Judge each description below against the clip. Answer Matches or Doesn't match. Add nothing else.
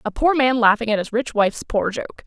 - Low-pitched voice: Doesn't match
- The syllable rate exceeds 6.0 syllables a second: Doesn't match